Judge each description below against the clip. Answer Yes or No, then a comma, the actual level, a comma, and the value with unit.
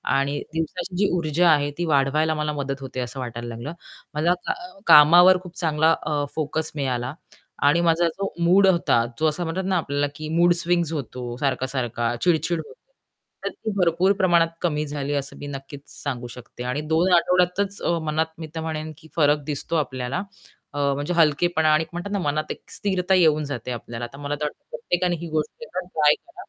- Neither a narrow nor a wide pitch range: Yes, average, 3.6 semitones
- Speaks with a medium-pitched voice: Yes, medium, 155 Hz